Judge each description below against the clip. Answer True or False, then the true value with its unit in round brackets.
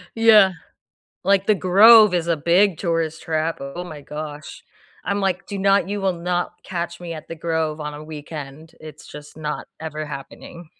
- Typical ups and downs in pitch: True (3.6 semitones)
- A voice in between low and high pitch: True (170 Hz)